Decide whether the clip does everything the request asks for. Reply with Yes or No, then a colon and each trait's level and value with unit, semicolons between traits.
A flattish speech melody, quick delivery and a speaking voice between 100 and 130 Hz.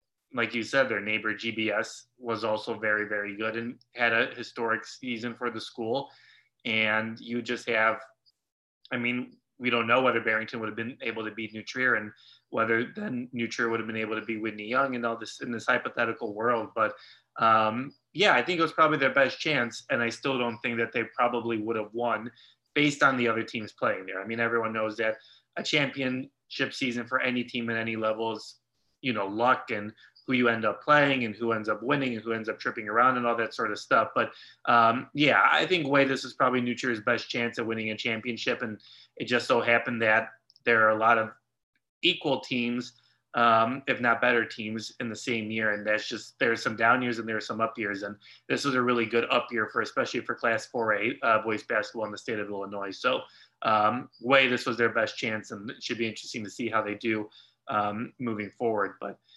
Yes: narrow, 1.9 semitones; fast, 220 wpm; low, 115 Hz